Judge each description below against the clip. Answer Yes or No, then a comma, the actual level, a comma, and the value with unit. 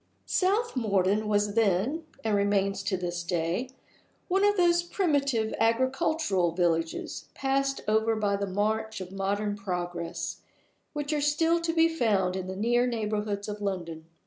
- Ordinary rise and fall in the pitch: No, wide, 6.2 semitones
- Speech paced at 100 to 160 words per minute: Yes, average, 145 wpm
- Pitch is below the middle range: No, high, 210 Hz